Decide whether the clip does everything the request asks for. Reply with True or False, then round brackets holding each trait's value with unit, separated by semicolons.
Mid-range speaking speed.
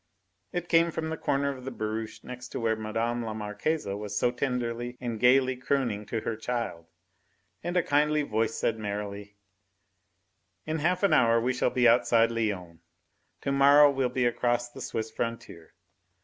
True (170 wpm)